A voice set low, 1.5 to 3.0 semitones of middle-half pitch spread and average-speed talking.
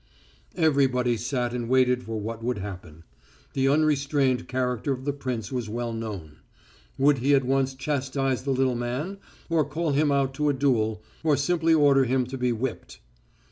Yes: low, 130 Hz; average, 2.7 semitones; average, 175 wpm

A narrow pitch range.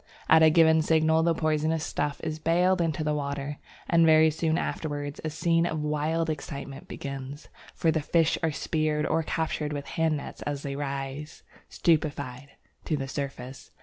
Yes: narrow, 2.0 semitones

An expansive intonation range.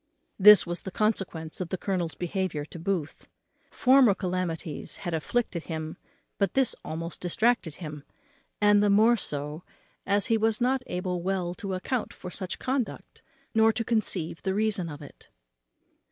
No: average, 4.4 semitones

